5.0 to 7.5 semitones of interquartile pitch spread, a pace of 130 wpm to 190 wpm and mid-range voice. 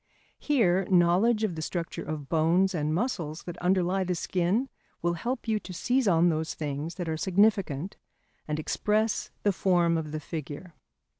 No: average, 3.7 semitones; average, 165 wpm; medium, 175 Hz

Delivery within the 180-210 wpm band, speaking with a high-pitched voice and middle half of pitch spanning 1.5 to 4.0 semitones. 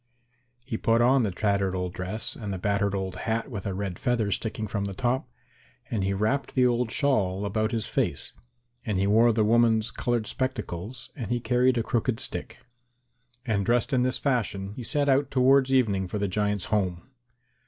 No: average, 190 wpm; low, 110 Hz; average, 3.7 semitones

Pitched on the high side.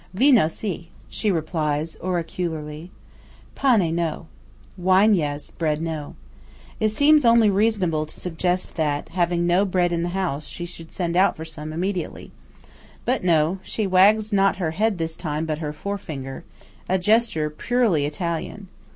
No: medium, 175 Hz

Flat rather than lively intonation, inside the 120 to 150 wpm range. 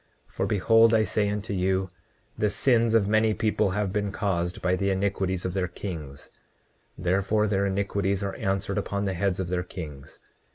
No: narrow, 2.0 semitones; average, 180 wpm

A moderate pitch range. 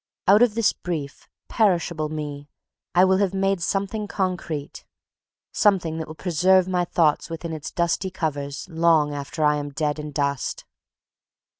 Yes: average, 4.0 semitones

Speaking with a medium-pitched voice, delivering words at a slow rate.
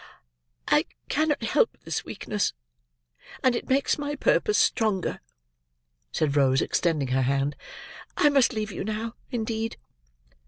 No: high, 220 Hz; slow, 125 wpm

